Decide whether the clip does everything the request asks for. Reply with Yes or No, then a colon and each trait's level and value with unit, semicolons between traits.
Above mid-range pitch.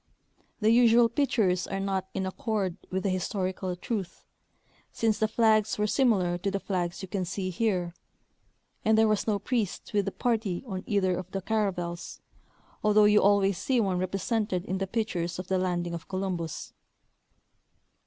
Yes: high, 195 Hz